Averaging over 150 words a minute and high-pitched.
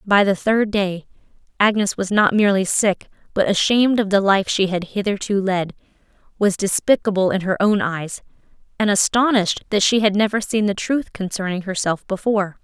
Yes: average, 170 wpm; high, 200 Hz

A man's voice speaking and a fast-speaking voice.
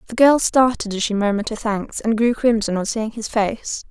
No: female; fast, 230 wpm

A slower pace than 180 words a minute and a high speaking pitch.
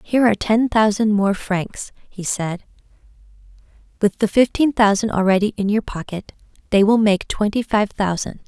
Yes: average, 155 wpm; high, 210 Hz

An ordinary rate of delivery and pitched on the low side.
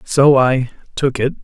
Yes: average, 165 wpm; low, 130 Hz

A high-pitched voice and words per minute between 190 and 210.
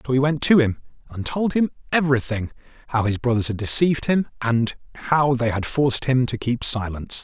No: low, 130 Hz; average, 200 wpm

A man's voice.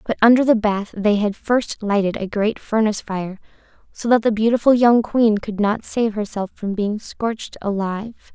No: female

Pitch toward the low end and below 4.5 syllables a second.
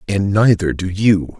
Yes: very low, 95 Hz; 4.1 syllables/s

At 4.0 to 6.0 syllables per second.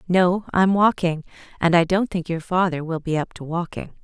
Yes: 5.0 syllables/s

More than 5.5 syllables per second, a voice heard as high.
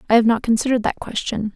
Yes: 7.4 syllables/s; high, 225 Hz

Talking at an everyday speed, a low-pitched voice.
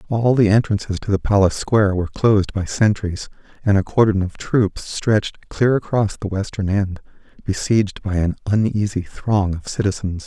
Yes: average, 170 wpm; low, 100 Hz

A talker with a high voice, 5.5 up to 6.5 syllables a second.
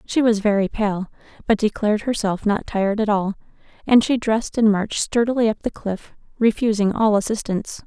Yes: high, 215 Hz; 5.6 syllables/s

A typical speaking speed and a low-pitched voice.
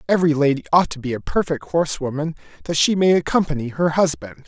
No: average, 190 wpm; medium, 155 Hz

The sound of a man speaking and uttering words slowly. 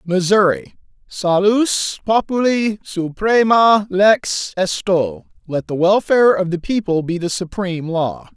Yes: male; slow, 110 wpm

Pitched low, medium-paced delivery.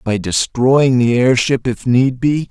Yes: low, 125 Hz; average, 170 wpm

